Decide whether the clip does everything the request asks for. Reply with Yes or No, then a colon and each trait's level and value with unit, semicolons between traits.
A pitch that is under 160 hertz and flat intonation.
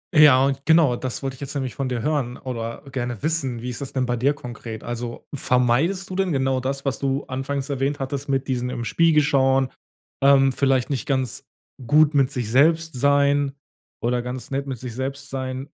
Yes: low, 135 Hz; narrow, 2.1 semitones